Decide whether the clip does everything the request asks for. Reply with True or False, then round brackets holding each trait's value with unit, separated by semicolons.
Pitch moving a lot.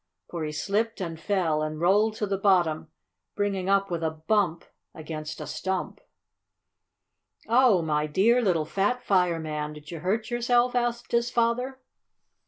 True (5.9 semitones)